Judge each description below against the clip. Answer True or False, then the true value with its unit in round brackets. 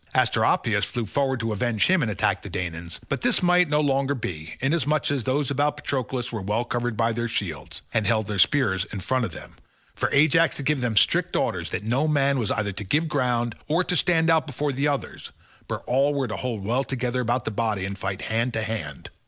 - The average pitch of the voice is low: True (125 Hz)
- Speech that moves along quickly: True (225 wpm)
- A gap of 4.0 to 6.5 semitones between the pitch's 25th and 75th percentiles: True (4.9 semitones)